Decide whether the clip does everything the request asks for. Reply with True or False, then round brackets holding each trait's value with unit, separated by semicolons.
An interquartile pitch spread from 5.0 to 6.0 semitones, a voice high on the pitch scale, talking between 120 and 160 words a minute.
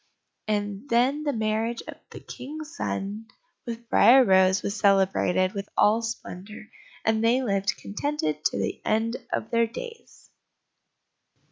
False (3.7 semitones; 220 Hz; 135 wpm)